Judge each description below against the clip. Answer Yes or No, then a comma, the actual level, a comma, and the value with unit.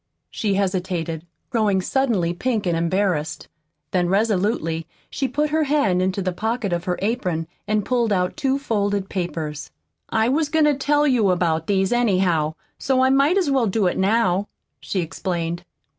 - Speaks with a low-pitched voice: No, high, 200 Hz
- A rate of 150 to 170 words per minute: Yes, average, 165 wpm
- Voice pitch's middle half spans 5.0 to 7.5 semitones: Yes, wide, 5.6 semitones